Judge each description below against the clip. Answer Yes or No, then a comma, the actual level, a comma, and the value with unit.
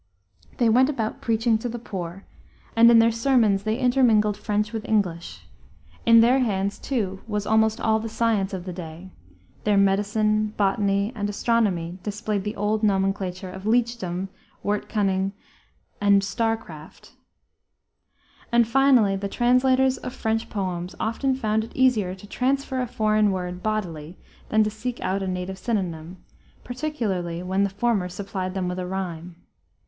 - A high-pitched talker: Yes, high, 210 Hz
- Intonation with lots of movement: No, average, 3.2 semitones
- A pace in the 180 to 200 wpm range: No, average, 155 wpm